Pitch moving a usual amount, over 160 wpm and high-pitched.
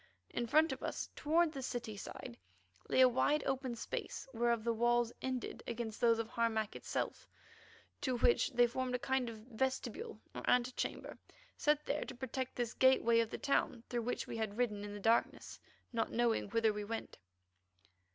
No: narrow, 2.3 semitones; average, 180 wpm; high, 240 Hz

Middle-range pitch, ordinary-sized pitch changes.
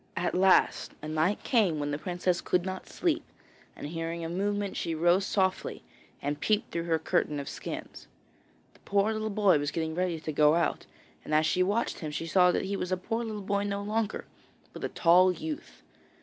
Yes: medium, 180 Hz; average, 3.8 semitones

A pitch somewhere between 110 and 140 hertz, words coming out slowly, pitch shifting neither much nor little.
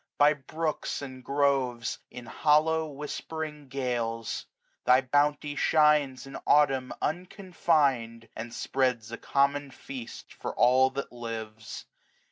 Yes: low, 135 Hz; slow, 110 wpm; average, 3.3 semitones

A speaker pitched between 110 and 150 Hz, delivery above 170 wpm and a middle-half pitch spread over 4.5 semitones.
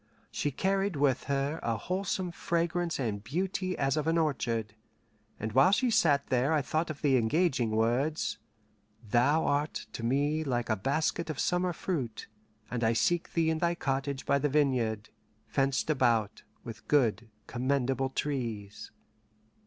No: medium, 140 Hz; average, 155 wpm; average, 5.1 semitones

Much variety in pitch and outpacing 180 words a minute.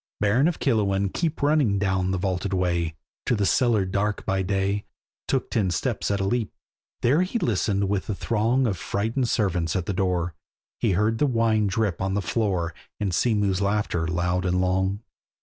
No: average, 3.3 semitones; average, 190 wpm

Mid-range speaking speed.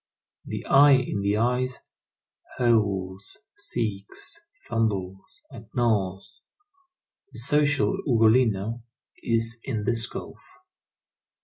No: slow, 90 wpm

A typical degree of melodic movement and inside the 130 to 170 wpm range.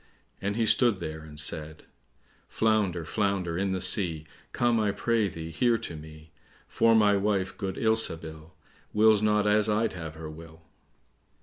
Yes: average, 5.0 semitones; average, 160 wpm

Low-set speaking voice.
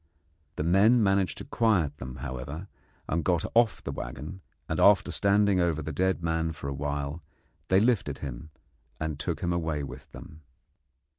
Yes: very low, 80 Hz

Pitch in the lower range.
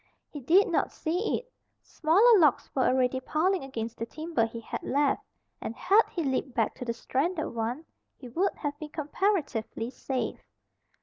No: very high, 285 Hz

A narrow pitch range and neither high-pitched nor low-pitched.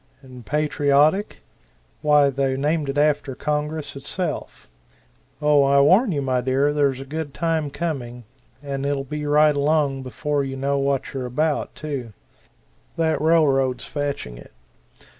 Yes: narrow, 1.9 semitones; medium, 145 Hz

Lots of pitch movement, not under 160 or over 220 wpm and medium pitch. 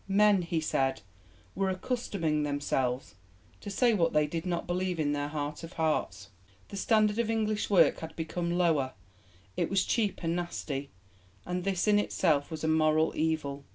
No: average, 4.5 semitones; average, 170 wpm; medium, 165 Hz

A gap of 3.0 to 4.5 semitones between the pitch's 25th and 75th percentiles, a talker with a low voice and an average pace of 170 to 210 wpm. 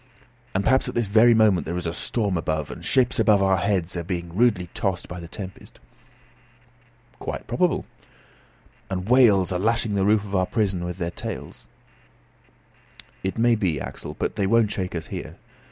Yes: average, 3.6 semitones; very low, 95 Hz; average, 180 wpm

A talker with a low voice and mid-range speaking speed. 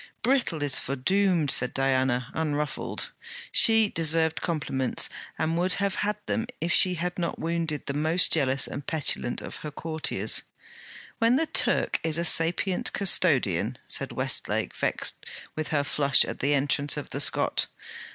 No: medium, 160 Hz; average, 150 wpm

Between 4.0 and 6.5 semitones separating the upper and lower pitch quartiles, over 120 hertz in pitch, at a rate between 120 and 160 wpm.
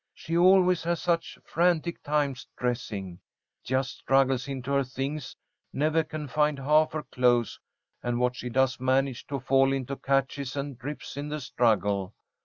No: average, 3.2 semitones; low, 135 Hz; average, 155 wpm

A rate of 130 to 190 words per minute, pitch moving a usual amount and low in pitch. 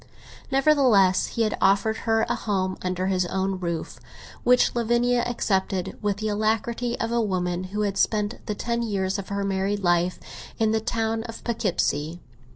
No: average, 165 wpm; average, 3.3 semitones; high, 205 Hz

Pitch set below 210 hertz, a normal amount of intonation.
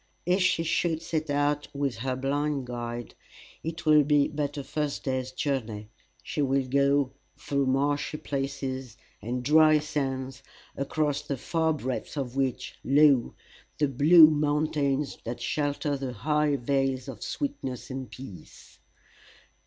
No: medium, 140 Hz; narrow, 2.3 semitones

